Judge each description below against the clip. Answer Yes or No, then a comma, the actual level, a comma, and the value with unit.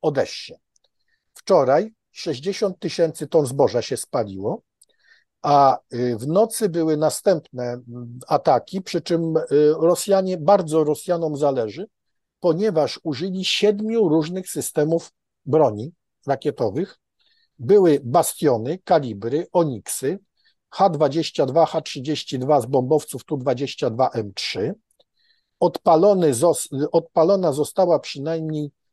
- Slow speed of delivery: Yes, slow, 80 wpm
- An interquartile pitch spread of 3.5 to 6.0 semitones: Yes, average, 4.2 semitones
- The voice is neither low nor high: Yes, medium, 160 Hz